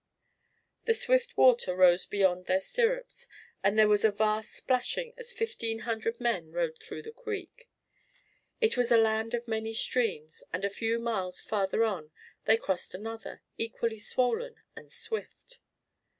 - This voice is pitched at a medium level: No, high, 230 Hz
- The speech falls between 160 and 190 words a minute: No, average, 150 wpm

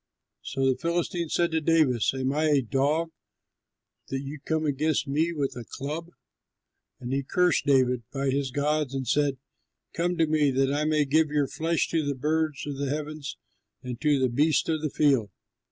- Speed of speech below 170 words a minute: No, average, 185 wpm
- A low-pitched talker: No, medium, 145 Hz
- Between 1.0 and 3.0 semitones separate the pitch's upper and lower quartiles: Yes, narrow, 2.6 semitones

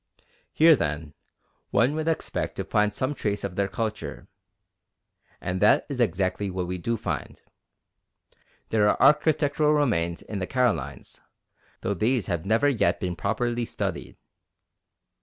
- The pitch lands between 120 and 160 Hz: No, low, 105 Hz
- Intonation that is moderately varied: No, wide, 6.0 semitones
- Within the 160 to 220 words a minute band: No, average, 140 wpm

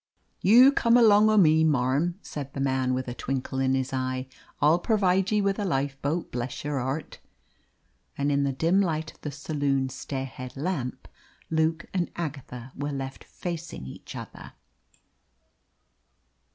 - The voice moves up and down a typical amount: Yes, average, 4.6 semitones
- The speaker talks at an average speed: Yes, average, 150 wpm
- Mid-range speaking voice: Yes, medium, 145 Hz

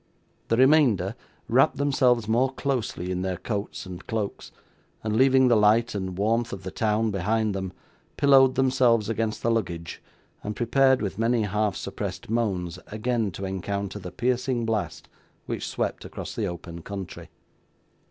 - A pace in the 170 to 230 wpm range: No, average, 150 wpm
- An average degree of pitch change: Yes, average, 4.0 semitones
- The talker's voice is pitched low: Yes, low, 110 Hz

